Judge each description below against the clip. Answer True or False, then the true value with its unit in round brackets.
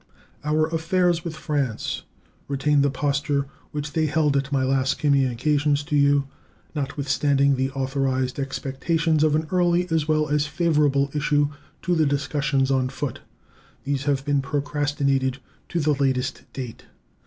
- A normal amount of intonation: False (1.9 semitones)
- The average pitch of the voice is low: False (145 Hz)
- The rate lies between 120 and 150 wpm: True (140 wpm)